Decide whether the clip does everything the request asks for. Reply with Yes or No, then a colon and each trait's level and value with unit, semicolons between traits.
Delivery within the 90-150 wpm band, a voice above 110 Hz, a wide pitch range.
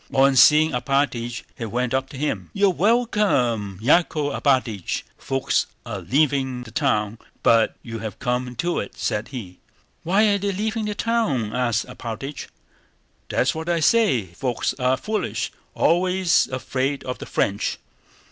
Yes: average, 145 wpm; low, 135 Hz; wide, 6.7 semitones